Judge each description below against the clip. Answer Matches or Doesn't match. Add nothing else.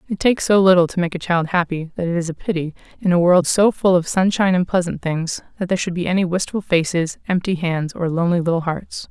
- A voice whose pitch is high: Doesn't match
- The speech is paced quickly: Matches